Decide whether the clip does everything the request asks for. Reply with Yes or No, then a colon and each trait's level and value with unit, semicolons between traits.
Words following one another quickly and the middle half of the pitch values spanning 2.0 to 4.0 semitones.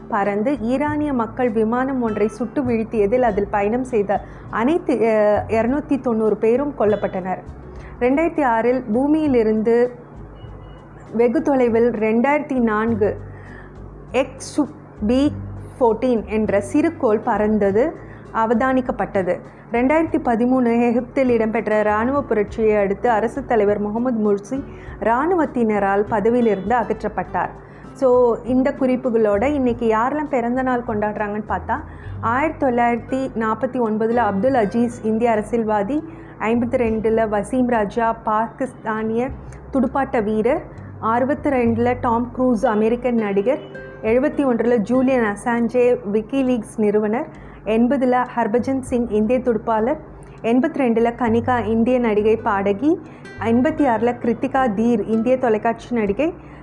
No: average, 105 wpm; average, 3.0 semitones